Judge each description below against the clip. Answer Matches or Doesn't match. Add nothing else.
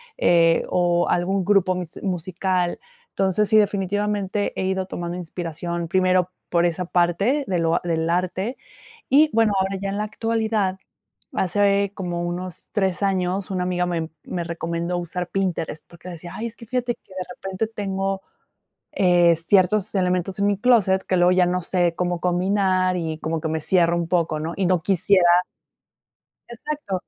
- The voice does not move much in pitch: Matches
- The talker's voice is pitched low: Doesn't match